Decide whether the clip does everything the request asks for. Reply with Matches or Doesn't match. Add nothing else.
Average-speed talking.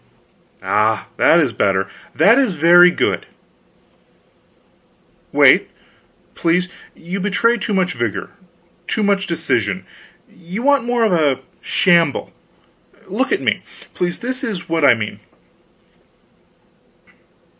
Doesn't match